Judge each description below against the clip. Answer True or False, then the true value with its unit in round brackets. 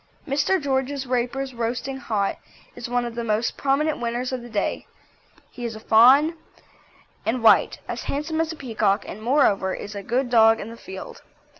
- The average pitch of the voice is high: True (245 Hz)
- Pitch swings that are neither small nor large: True (3.4 semitones)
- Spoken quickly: False (180 wpm)